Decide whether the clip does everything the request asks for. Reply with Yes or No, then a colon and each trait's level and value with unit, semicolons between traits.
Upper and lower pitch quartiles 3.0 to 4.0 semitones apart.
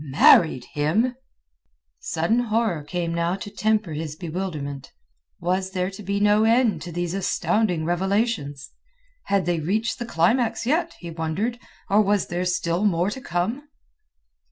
No: average, 4.5 semitones